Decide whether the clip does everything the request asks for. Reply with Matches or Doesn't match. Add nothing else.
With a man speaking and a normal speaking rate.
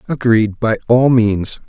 Matches